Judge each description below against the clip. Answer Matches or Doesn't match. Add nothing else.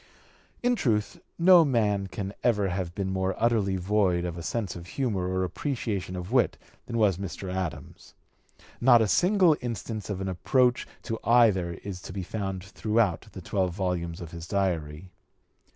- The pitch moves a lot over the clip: Doesn't match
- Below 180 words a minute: Matches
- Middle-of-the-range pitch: Doesn't match